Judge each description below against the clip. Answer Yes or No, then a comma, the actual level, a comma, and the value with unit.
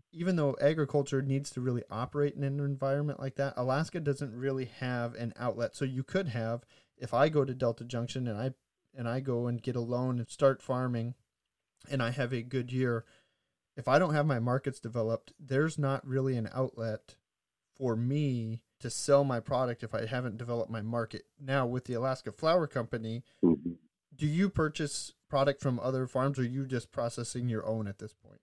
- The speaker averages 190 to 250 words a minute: Yes, average, 195 wpm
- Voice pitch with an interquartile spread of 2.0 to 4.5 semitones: Yes, average, 2.9 semitones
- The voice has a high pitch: No, low, 130 Hz